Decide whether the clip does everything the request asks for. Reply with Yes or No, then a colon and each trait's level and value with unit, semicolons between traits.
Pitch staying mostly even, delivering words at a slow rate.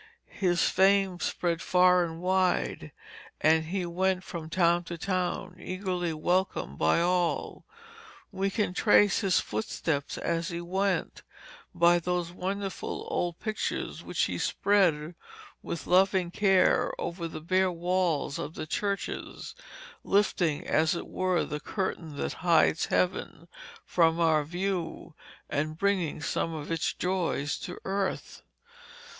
Yes: narrow, 2.3 semitones; slow, 130 wpm